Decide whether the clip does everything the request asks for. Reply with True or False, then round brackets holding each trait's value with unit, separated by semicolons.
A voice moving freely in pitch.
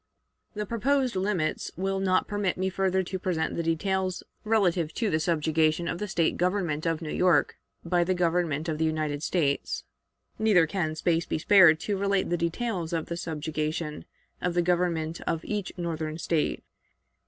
False (3.0 semitones)